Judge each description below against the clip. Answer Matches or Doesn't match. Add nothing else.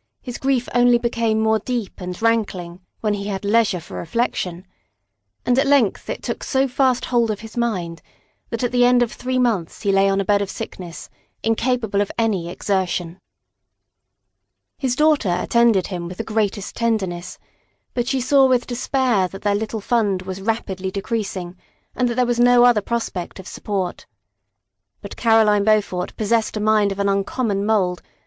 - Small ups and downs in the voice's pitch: Doesn't match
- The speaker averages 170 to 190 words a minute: Matches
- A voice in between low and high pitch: Doesn't match